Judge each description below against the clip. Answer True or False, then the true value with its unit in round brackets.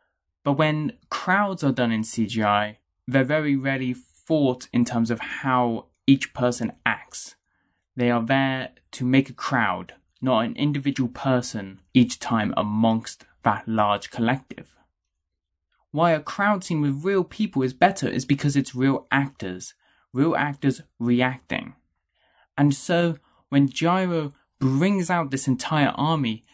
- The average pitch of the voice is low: True (130 Hz)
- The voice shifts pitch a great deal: False (3.7 semitones)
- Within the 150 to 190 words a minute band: False (140 wpm)